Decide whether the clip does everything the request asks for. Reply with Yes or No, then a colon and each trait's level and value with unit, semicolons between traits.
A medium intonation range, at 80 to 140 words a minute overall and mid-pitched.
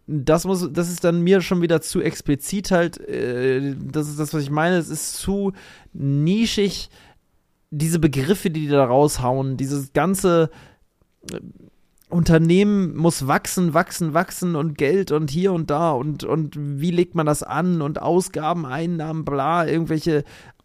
No: average, 3.1 semitones; average, 150 wpm; medium, 160 Hz